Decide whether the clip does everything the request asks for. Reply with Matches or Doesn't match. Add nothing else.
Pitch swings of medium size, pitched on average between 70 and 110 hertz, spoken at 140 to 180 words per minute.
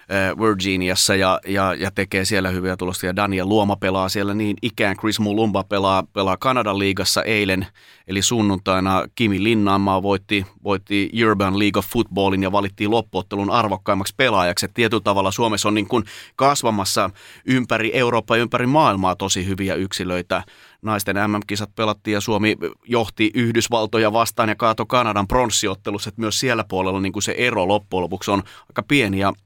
Doesn't match